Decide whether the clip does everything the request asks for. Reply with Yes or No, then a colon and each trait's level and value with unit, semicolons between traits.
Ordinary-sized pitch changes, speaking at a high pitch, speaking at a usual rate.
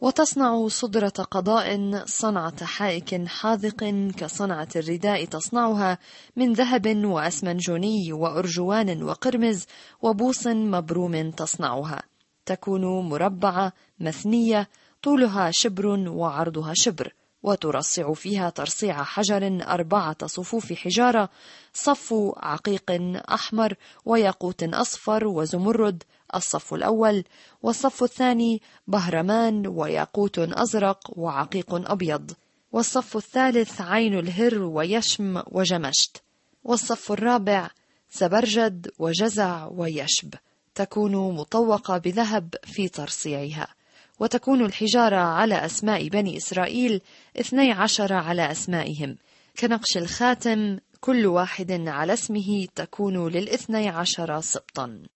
Yes: average, 4.2 semitones; high, 200 Hz; average, 90 wpm